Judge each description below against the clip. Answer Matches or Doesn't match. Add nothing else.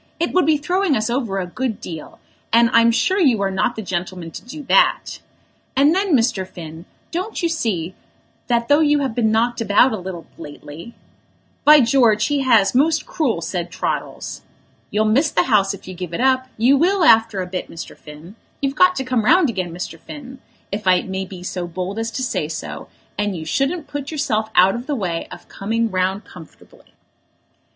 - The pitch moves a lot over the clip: Matches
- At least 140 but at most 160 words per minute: Doesn't match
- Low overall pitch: Doesn't match